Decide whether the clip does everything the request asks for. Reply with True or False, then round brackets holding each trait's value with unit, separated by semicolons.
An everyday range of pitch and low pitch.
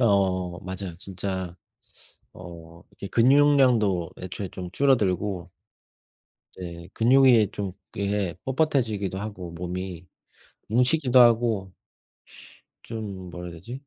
True (4.6 semitones; 100 Hz)